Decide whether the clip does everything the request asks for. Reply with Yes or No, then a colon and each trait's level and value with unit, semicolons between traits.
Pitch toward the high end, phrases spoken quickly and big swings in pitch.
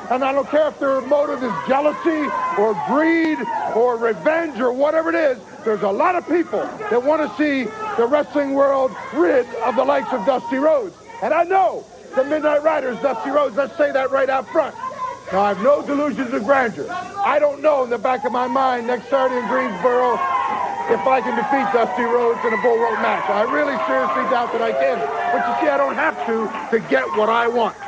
No: very high, 275 Hz; fast, 215 wpm; average, 3.7 semitones